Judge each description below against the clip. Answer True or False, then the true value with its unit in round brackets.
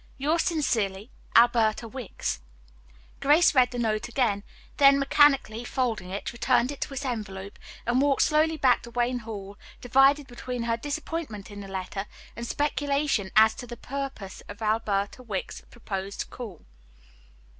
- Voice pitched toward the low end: False (240 Hz)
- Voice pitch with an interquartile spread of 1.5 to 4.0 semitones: False (4.5 semitones)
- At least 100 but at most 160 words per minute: True (145 wpm)